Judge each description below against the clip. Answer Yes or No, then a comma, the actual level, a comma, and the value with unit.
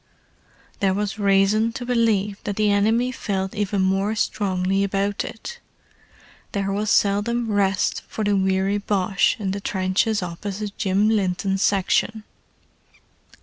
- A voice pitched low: No, high, 200 Hz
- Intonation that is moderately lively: No, narrow, 1.8 semitones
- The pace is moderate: No, slow, 125 wpm